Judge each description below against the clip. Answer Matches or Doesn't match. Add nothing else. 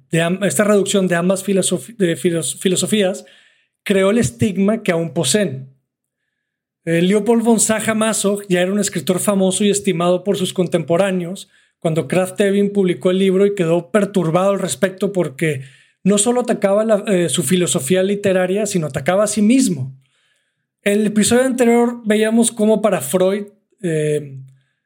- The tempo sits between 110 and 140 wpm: Doesn't match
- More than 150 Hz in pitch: Matches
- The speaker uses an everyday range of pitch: Matches